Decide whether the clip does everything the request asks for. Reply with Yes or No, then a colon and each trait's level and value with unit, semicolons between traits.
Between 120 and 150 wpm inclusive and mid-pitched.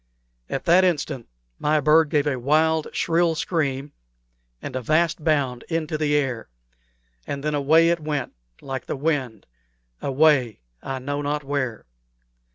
Yes: average, 145 wpm; medium, 145 Hz